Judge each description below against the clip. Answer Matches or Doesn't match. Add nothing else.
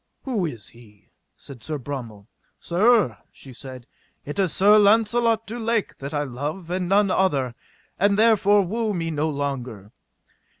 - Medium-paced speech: Matches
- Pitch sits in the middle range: Matches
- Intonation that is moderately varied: Doesn't match